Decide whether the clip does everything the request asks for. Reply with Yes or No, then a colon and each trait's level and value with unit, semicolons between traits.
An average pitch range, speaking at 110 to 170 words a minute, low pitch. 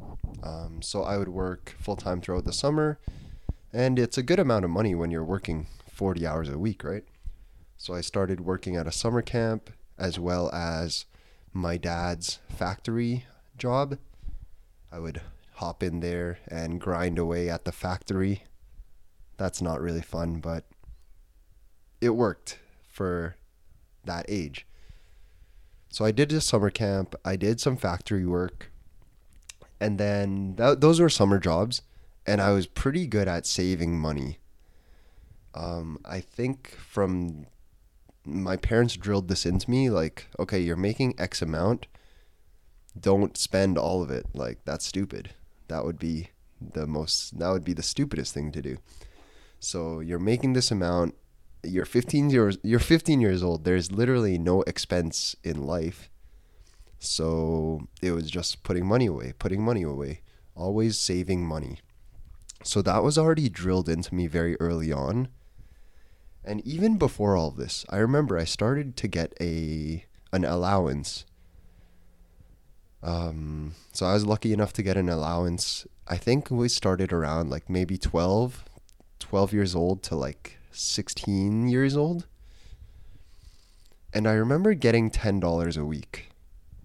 Yes: average, 4.0 semitones; average, 145 wpm; very low, 90 Hz